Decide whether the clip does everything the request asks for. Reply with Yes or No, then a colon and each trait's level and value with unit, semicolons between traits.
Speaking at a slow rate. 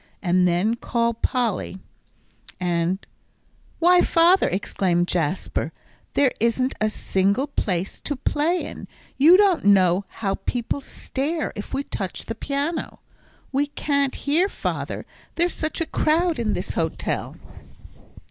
Yes: slow, 130 wpm